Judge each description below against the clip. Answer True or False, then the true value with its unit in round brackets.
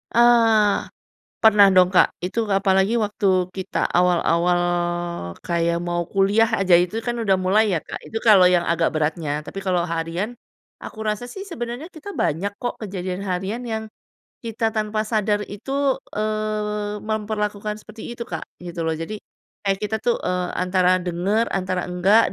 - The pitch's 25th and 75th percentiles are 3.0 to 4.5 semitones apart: True (3.3 semitones)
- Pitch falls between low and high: False (200 Hz)